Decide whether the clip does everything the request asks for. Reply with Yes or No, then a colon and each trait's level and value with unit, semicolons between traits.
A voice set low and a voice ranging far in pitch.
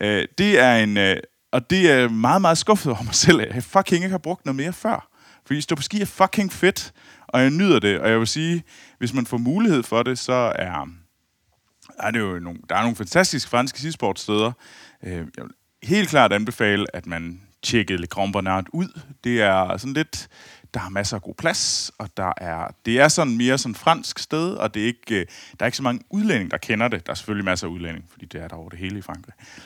Yes: low, 120 Hz; wide, 8.0 semitones